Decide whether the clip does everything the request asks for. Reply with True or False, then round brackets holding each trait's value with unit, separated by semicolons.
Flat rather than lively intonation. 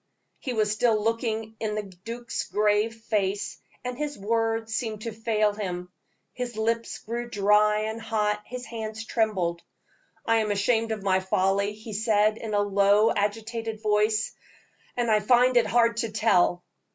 True (1.6 semitones)